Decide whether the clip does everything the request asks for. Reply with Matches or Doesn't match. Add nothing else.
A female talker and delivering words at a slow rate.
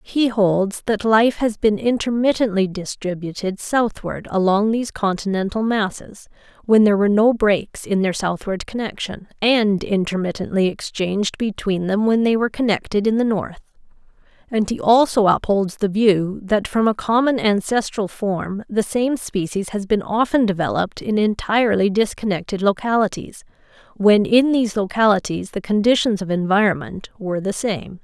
Doesn't match